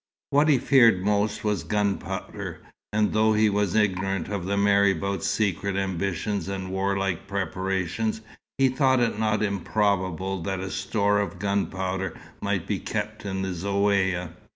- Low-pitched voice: Yes, low, 100 Hz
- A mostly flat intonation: Yes, narrow, 1.8 semitones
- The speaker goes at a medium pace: Yes, average, 145 wpm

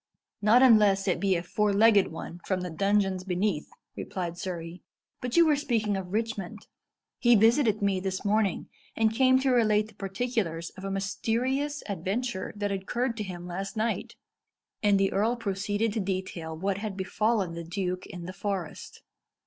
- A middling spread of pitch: Yes, average, 3.1 semitones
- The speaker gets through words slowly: No, average, 170 wpm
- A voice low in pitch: No, high, 200 Hz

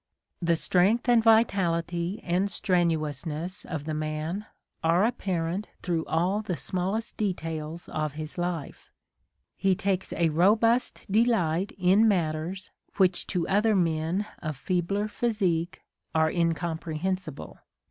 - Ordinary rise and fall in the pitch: Yes, average, 3.6 semitones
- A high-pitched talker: No, medium, 175 Hz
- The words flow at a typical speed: No, slow, 115 wpm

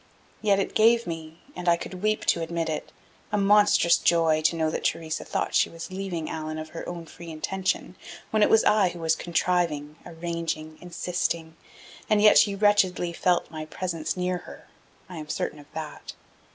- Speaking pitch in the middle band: Yes, medium, 170 Hz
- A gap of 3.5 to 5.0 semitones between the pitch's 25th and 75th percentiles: No, average, 2.8 semitones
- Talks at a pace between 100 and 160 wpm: No, average, 185 wpm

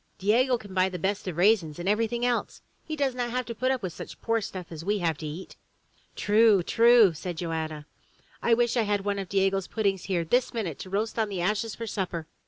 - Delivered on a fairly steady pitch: No, average, 4.3 semitones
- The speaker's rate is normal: No, fast, 230 wpm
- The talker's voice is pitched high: Yes, high, 200 Hz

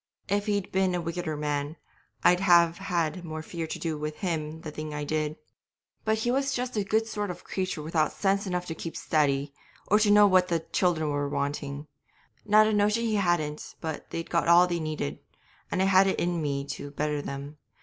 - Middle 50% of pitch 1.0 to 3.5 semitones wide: No, average, 4.3 semitones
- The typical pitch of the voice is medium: Yes, medium, 170 Hz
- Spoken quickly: Yes, fast, 210 wpm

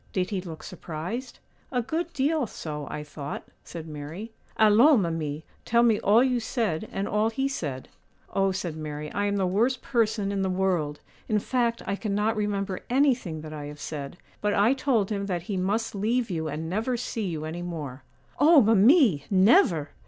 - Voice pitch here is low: No, high, 200 Hz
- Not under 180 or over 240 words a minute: Yes, average, 185 wpm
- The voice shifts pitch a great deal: Yes, wide, 6.2 semitones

